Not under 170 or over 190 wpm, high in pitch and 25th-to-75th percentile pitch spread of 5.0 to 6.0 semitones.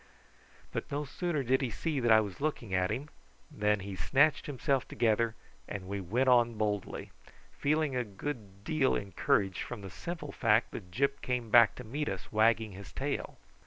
No: average, 180 wpm; low, 115 Hz; wide, 5.4 semitones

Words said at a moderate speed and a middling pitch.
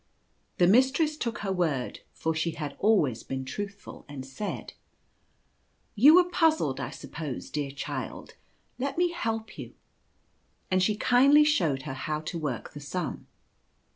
Yes: average, 160 wpm; medium, 180 Hz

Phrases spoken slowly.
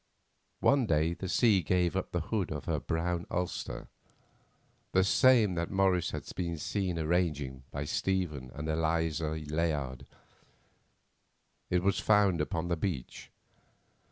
Yes: slow, 130 wpm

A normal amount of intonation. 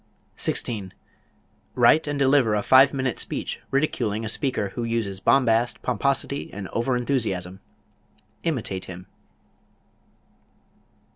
Yes: average, 4.7 semitones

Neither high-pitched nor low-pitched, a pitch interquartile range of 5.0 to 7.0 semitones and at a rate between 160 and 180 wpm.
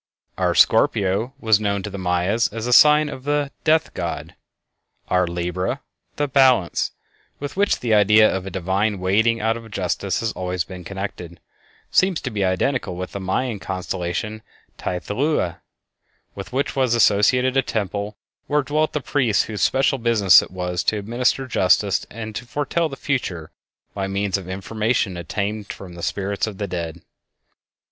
No: low, 105 Hz; average, 5.3 semitones; average, 165 wpm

